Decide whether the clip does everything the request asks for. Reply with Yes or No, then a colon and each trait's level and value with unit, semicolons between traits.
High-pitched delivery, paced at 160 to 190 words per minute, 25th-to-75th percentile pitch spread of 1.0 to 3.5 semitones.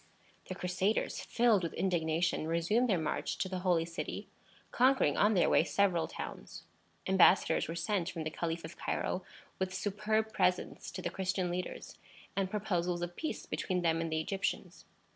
No: medium, 180 Hz; average, 165 wpm; average, 2.9 semitones